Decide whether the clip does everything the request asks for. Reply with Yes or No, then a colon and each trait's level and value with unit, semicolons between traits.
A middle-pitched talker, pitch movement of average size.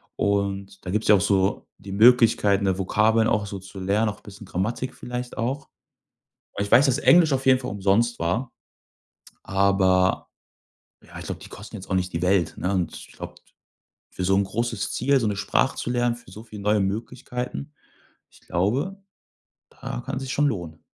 No: low, 105 Hz; average, 4.0 semitones